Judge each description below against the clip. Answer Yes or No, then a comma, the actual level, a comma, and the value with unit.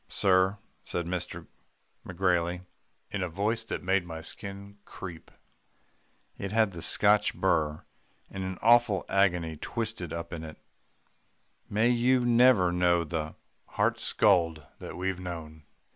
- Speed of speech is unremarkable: No, slow, 130 wpm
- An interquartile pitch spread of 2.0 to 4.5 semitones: Yes, average, 3.3 semitones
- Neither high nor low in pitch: No, very low, 90 Hz